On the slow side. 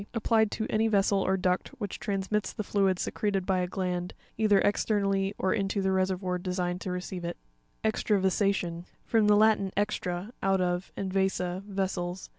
No: average, 165 wpm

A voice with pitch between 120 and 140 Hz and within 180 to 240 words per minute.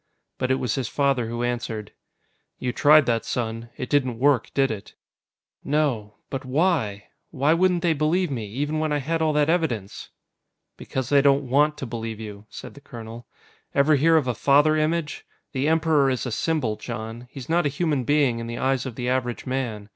Yes: low, 135 Hz; average, 195 wpm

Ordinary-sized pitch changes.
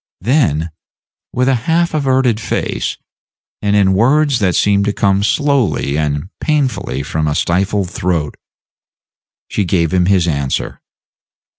No: wide, 7.1 semitones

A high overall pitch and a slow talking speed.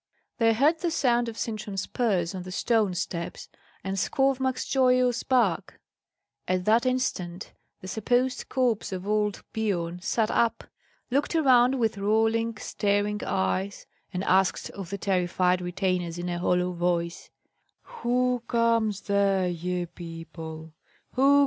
Yes: high, 200 Hz; slow, 130 wpm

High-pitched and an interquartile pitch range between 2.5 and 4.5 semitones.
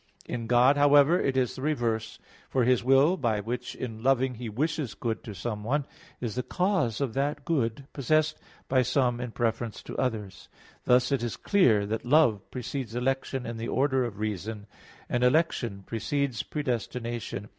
No: low, 125 Hz; average, 3.4 semitones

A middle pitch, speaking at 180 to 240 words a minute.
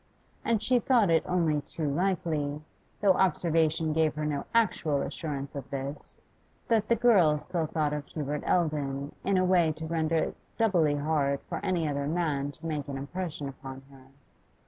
No: medium, 155 Hz; average, 170 wpm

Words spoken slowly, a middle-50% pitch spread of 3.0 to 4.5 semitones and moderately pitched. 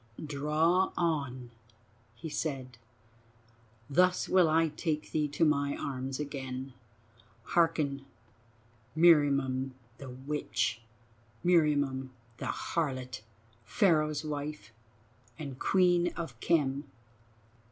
Yes: slow, 85 wpm; average, 3.5 semitones; medium, 145 Hz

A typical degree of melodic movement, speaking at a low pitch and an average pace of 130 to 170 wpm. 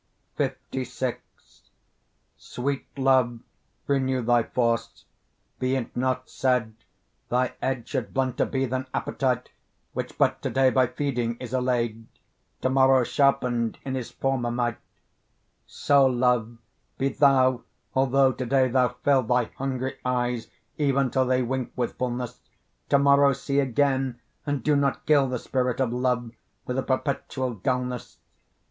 No: narrow, 1.5 semitones; low, 130 Hz; average, 140 wpm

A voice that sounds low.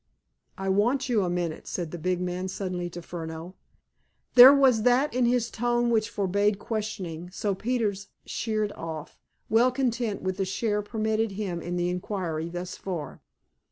No: high, 200 Hz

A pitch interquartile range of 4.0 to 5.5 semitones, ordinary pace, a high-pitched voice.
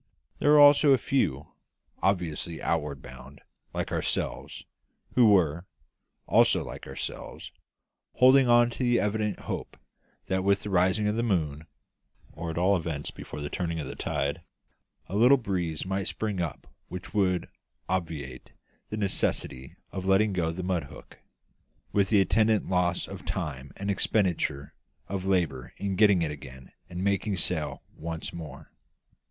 No: average, 4.7 semitones; average, 150 wpm; very low, 90 Hz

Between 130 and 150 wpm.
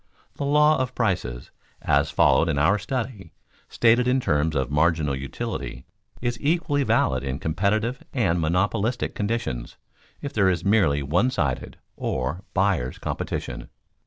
Yes: average, 140 wpm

